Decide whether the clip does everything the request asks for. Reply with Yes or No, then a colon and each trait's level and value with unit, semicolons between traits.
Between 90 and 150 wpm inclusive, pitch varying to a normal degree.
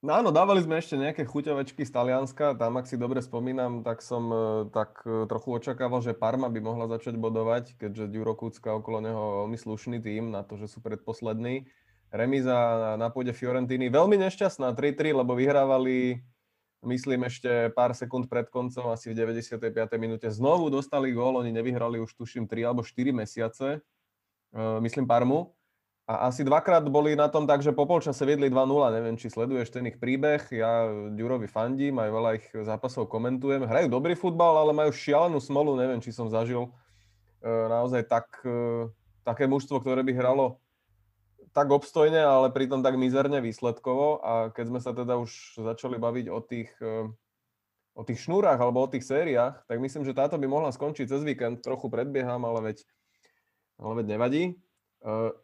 No: fast, 165 wpm; average, 3.1 semitones